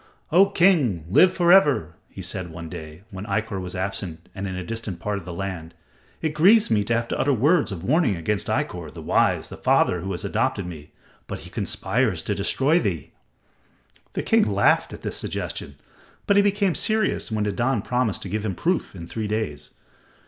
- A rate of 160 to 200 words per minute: Yes, average, 195 wpm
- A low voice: Yes, low, 105 Hz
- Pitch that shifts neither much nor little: No, wide, 8.3 semitones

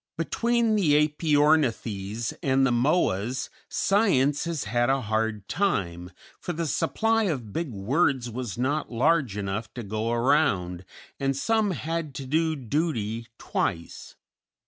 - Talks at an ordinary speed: No, slow, 130 wpm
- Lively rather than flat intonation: Yes, wide, 6.2 semitones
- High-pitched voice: No, low, 135 Hz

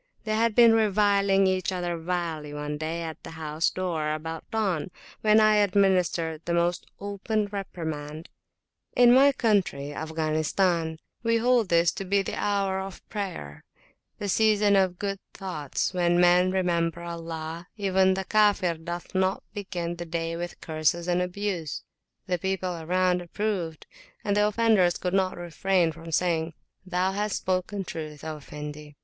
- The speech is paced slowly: No, average, 155 wpm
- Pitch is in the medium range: Yes, medium, 180 Hz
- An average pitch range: Yes, average, 3.4 semitones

